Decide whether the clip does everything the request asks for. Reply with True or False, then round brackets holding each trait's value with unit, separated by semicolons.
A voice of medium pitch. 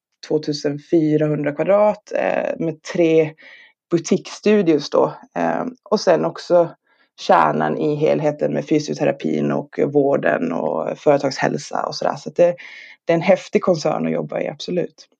True (155 Hz)